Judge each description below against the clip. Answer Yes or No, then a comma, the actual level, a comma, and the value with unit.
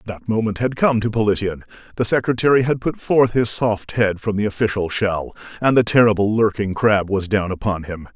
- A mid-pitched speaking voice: No, low, 105 Hz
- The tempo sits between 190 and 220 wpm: Yes, average, 200 wpm